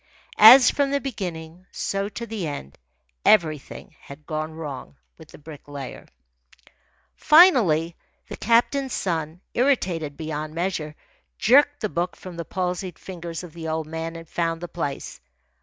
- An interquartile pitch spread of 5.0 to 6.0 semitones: No, average, 4.5 semitones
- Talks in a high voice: No, medium, 170 Hz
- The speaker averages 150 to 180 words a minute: No, average, 140 wpm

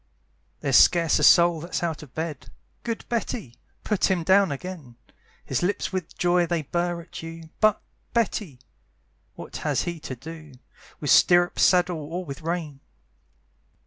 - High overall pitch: No, medium, 170 Hz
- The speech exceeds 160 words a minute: No, average, 150 wpm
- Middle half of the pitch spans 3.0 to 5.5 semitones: No, narrow, 2.6 semitones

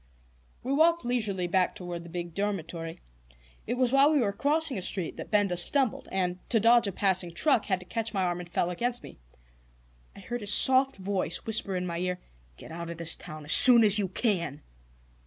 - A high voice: Yes, high, 195 Hz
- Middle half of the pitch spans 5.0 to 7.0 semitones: Yes, average, 5.3 semitones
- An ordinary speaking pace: No, fast, 210 wpm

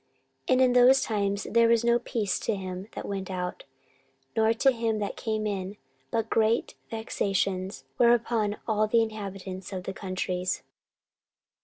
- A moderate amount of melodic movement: Yes, average, 3.1 semitones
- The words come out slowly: No, average, 160 wpm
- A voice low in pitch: No, high, 215 Hz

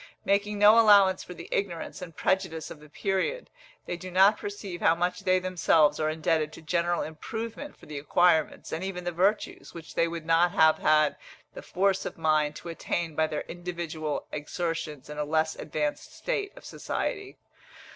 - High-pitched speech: No, medium, 170 Hz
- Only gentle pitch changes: No, average, 3.4 semitones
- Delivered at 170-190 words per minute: Yes, average, 180 wpm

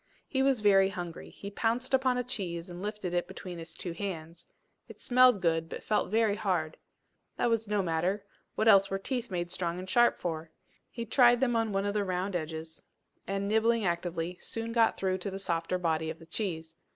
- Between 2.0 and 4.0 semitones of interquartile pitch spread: No, average, 4.7 semitones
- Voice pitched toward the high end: Yes, high, 195 Hz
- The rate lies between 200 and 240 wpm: Yes, fast, 205 wpm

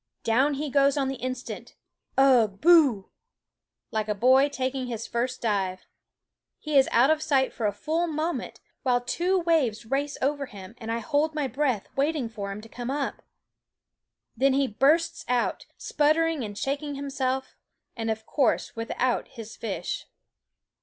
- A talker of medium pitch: No, very high, 265 Hz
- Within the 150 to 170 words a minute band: Yes, average, 160 wpm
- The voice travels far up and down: No, average, 4.3 semitones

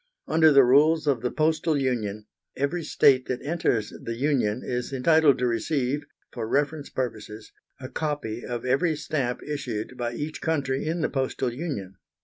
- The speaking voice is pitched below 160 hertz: Yes, low, 135 Hz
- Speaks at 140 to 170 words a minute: Yes, average, 160 wpm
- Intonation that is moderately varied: Yes, average, 4.0 semitones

